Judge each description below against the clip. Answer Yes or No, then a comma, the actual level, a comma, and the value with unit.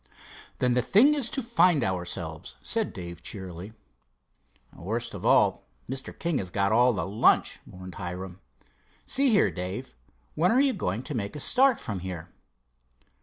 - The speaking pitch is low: Yes, low, 105 Hz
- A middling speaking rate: Yes, average, 160 wpm